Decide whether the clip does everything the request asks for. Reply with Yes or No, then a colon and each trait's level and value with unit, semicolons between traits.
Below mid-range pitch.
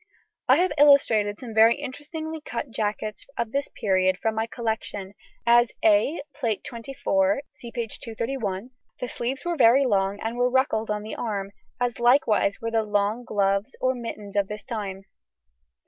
No: high, 230 Hz